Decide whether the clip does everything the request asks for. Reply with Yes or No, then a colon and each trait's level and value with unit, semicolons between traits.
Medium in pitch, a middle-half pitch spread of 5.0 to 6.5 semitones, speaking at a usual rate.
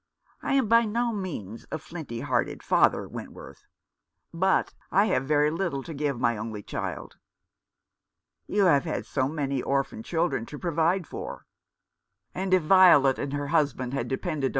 Yes: medium, 155 Hz; wide, 5.5 semitones; average, 160 wpm